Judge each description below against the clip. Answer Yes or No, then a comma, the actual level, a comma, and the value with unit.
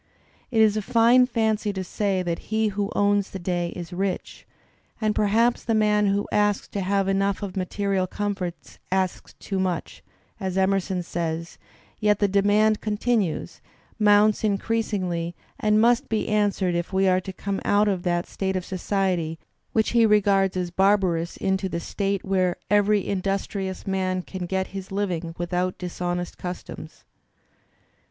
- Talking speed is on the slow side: No, average, 160 wpm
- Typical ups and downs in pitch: No, narrow, 2.2 semitones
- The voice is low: No, high, 195 Hz